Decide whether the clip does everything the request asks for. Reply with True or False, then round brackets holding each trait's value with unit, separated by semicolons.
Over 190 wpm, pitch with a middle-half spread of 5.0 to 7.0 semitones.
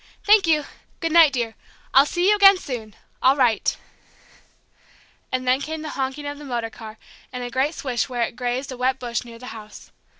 False (200 wpm; 3.7 semitones)